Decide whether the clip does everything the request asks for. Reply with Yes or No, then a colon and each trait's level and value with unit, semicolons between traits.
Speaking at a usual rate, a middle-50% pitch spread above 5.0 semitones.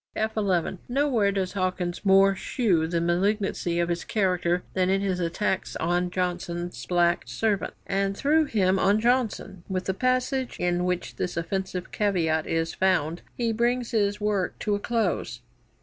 No: average, 165 wpm; average, 3.1 semitones